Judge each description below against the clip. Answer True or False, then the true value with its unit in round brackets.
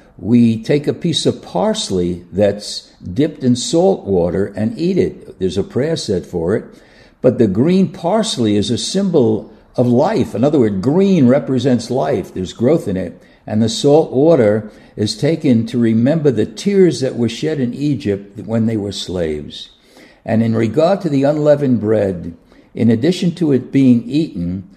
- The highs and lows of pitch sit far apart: True (6.1 semitones)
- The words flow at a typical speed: True (170 wpm)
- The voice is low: True (120 Hz)